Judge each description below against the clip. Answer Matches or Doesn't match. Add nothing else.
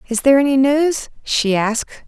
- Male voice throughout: Doesn't match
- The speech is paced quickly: Doesn't match